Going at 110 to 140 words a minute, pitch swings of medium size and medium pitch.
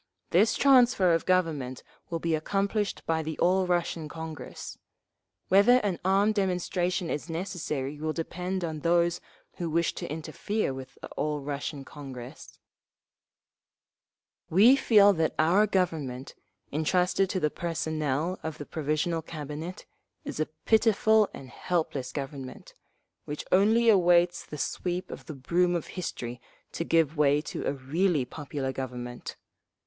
Yes: slow, 135 wpm; average, 3.8 semitones; medium, 165 Hz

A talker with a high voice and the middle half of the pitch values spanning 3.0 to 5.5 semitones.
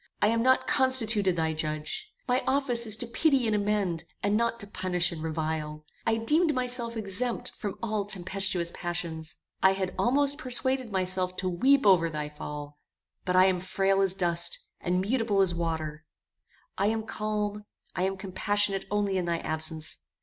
Yes: high, 195 Hz; average, 4.7 semitones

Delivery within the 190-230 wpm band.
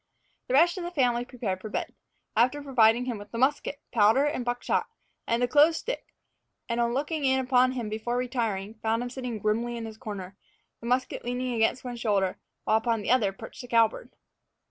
Yes: fast, 205 wpm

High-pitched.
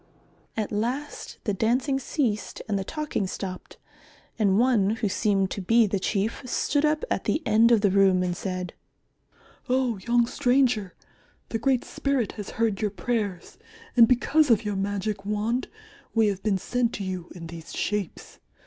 Yes: high, 215 Hz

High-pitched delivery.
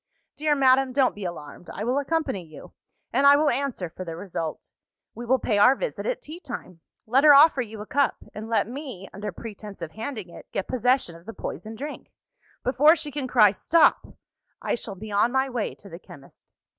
Yes: high, 235 Hz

